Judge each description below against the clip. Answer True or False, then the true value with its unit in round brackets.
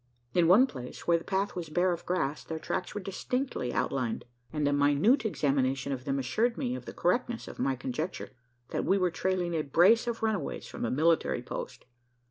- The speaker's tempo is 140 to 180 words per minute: False (200 wpm)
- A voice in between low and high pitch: True (170 Hz)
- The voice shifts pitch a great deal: True (6.2 semitones)